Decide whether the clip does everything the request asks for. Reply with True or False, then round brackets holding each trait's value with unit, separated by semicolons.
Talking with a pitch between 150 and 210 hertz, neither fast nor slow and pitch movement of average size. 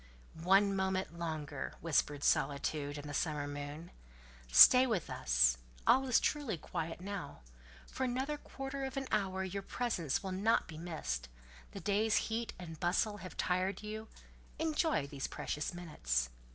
False (185 Hz; 150 wpm; 6.7 semitones)